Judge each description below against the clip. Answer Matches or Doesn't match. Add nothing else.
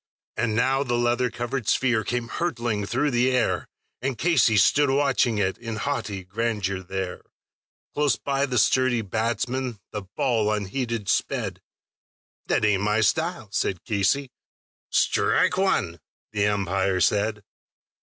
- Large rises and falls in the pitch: Doesn't match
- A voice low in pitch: Matches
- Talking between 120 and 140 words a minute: Matches